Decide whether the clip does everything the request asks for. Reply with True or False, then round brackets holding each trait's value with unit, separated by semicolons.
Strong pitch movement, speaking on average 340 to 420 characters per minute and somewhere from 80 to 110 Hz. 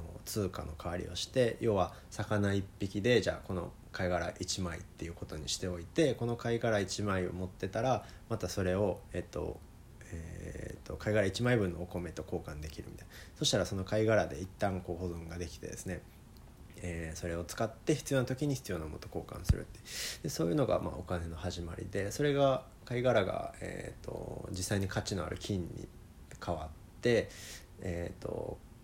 False (3.7 semitones; 345 characters per minute; 95 Hz)